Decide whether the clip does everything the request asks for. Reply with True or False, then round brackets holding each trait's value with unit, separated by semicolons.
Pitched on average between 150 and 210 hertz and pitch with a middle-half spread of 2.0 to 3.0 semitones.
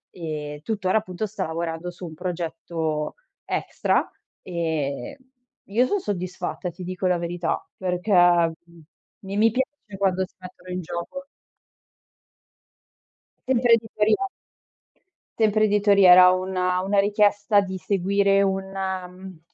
True (185 Hz; 2.7 semitones)